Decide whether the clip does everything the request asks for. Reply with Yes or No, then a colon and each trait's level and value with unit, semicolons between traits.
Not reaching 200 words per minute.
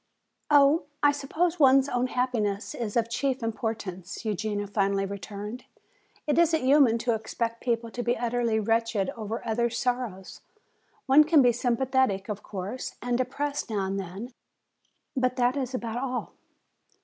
Yes: average, 150 wpm